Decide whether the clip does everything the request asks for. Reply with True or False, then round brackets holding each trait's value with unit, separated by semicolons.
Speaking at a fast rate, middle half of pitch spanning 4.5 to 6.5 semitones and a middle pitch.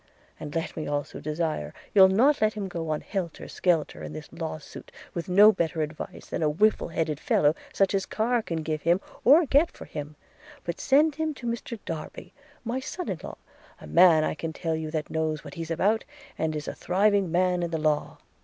True (210 wpm; 5.2 semitones; 170 Hz)